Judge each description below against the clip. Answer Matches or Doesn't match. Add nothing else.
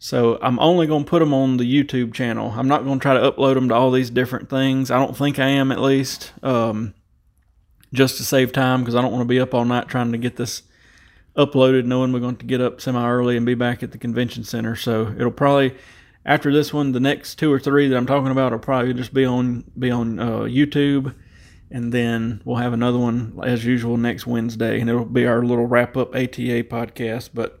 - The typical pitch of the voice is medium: Doesn't match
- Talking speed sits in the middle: Doesn't match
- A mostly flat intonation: Matches